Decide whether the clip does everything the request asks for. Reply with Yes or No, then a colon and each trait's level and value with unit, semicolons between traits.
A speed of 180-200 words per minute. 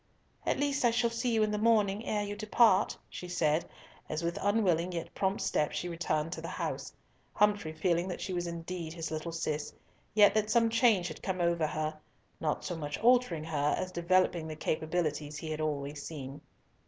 Yes: average, 195 wpm